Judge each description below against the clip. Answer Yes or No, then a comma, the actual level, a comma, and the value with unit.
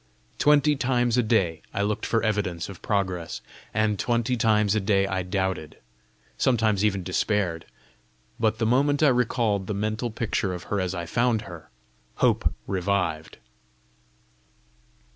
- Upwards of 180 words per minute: No, average, 145 wpm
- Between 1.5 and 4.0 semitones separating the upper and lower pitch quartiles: Yes, average, 3.7 semitones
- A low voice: Yes, low, 105 Hz